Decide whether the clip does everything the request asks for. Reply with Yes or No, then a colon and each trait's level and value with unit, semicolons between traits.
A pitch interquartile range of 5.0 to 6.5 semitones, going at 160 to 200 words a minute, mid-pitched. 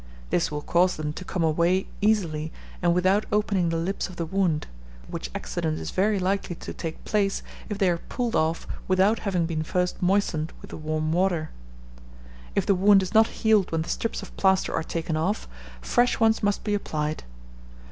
No: average, 3.7 semitones; average, 190 wpm; medium, 180 Hz